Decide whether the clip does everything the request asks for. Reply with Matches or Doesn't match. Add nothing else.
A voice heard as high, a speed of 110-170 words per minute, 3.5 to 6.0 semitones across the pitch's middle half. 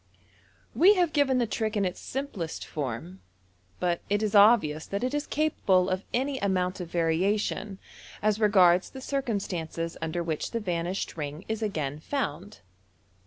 Matches